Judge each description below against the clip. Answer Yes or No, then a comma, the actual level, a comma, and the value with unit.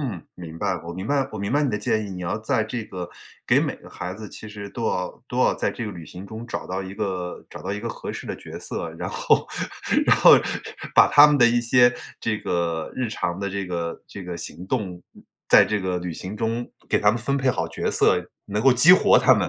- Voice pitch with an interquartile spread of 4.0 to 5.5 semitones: Yes, average, 4.6 semitones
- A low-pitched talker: Yes, low, 105 Hz